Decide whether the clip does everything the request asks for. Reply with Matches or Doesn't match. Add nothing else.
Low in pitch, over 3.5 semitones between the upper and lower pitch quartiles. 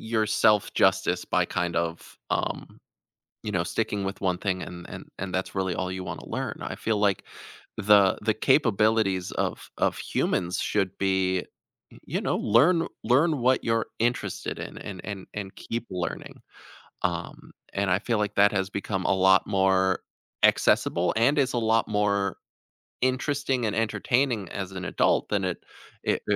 Doesn't match